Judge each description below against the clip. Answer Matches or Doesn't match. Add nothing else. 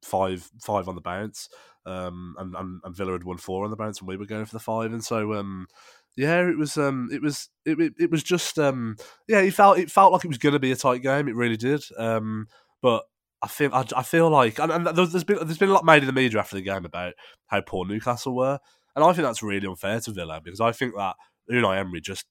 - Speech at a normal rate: Doesn't match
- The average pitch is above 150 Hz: Doesn't match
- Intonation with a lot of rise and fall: Matches